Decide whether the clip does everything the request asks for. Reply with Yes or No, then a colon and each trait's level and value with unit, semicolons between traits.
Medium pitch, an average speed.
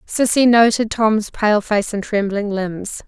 No: high, 215 Hz; average, 155 wpm